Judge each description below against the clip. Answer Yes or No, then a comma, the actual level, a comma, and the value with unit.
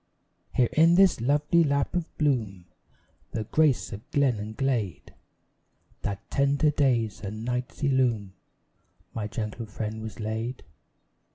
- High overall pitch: No, low, 125 Hz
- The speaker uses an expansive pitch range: No, average, 4.7 semitones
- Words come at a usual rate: No, slow, 125 wpm